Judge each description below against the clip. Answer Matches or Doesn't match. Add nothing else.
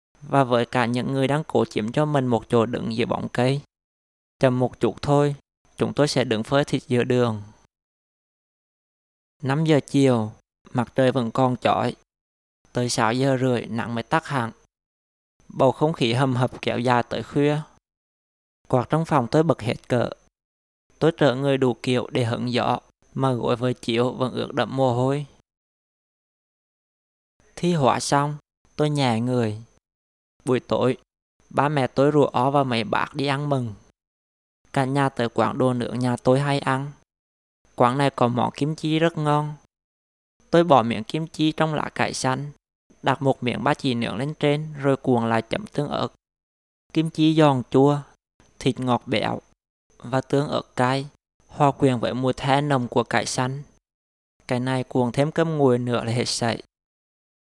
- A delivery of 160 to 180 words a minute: Matches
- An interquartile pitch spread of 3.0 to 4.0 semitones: Matches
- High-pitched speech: Doesn't match